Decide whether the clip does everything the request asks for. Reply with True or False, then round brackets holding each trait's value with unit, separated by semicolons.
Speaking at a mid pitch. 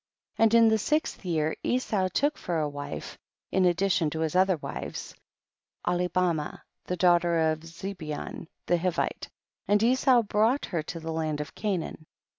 True (175 Hz)